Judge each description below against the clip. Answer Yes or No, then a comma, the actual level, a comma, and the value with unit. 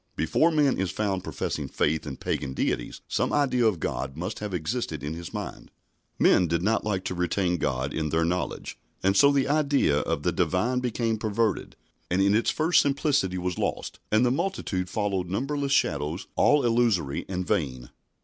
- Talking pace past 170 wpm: Yes, average, 180 wpm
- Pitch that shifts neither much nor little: No, wide, 6.5 semitones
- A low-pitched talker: Yes, very low, 95 Hz